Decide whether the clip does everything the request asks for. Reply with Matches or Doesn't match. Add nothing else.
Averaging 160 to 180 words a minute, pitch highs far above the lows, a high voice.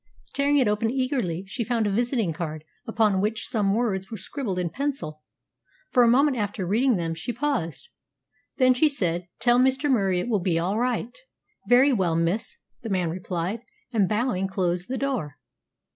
Matches